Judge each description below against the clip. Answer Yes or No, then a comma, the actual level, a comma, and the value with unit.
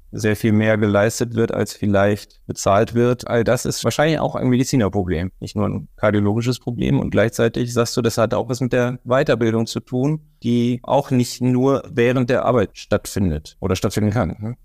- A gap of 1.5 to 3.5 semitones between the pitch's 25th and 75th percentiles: Yes, average, 3.2 semitones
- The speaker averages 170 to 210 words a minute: Yes, fast, 190 wpm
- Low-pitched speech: Yes, low, 115 Hz